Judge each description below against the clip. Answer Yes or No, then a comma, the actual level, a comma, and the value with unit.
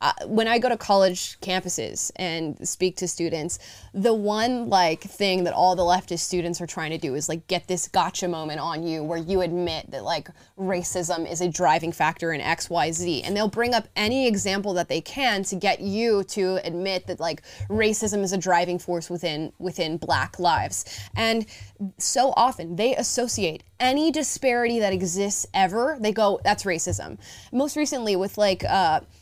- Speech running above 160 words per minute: Yes, average, 185 wpm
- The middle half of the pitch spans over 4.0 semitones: No, average, 3.7 semitones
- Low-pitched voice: No, medium, 185 Hz